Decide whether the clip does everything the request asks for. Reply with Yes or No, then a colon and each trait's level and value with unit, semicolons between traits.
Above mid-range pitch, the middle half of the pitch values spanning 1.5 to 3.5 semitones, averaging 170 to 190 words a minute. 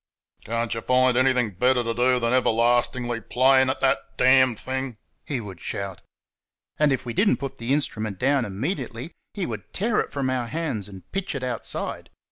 No: low, 125 Hz; narrow, 2.6 semitones; average, 185 wpm